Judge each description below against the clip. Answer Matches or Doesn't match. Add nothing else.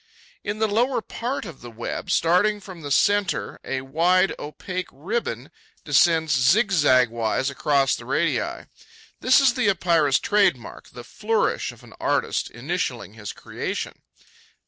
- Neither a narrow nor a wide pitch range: Doesn't match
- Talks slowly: Doesn't match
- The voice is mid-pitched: Matches